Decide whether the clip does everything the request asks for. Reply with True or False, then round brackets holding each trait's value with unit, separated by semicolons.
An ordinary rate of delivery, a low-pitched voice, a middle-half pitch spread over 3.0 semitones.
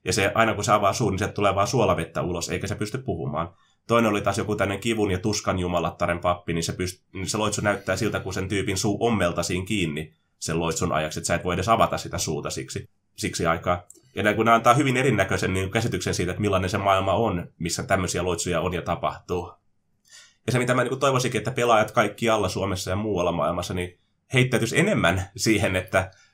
False (210 wpm; 100 Hz; 3.6 semitones)